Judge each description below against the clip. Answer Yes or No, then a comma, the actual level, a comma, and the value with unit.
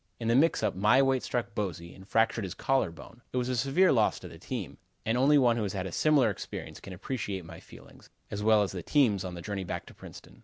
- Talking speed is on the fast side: Yes, fast, 255 wpm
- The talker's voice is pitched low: Yes, low, 110 Hz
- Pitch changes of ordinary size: Yes, average, 4.9 semitones